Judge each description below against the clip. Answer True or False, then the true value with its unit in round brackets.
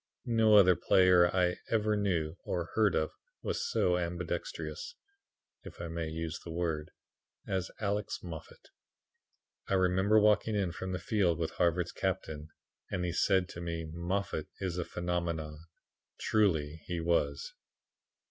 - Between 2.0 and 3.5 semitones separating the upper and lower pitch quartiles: True (2.9 semitones)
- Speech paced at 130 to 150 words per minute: True (140 wpm)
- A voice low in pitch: True (90 Hz)